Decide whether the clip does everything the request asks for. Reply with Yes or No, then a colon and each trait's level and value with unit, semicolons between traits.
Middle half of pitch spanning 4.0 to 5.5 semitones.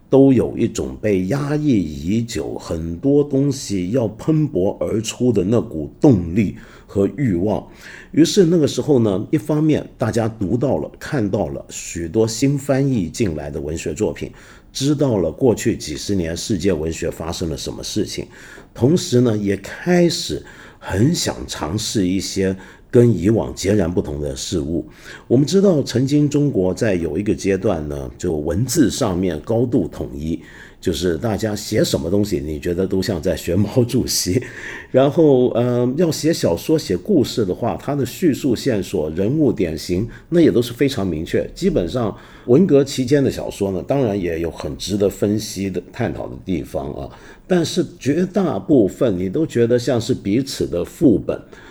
No: wide, 6.8 semitones